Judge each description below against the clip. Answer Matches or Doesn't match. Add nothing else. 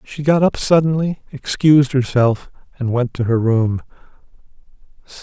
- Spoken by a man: Matches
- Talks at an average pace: Doesn't match